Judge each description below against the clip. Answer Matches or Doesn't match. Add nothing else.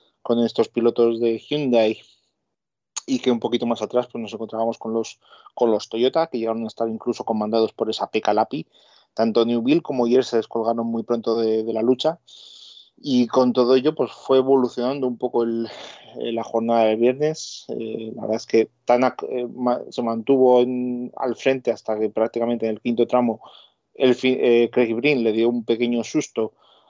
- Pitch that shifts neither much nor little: Doesn't match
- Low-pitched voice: Matches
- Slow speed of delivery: Doesn't match